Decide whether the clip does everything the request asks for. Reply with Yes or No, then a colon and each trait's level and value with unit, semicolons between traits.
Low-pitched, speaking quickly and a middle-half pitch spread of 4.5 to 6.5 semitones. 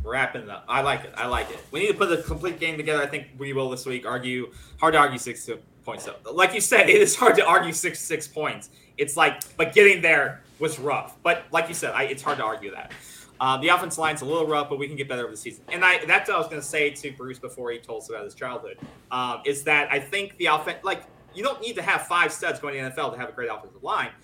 No: medium, 150 Hz; fast, 290 wpm; average, 5.0 semitones